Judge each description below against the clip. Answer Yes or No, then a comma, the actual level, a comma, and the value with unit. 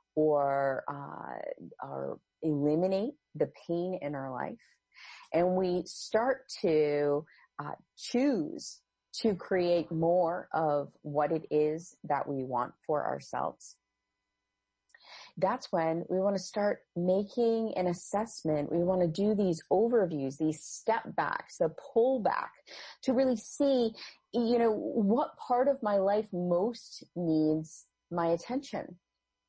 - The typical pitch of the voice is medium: Yes, medium, 175 Hz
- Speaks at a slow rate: Yes, slow, 120 wpm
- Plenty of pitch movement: Yes, wide, 6.5 semitones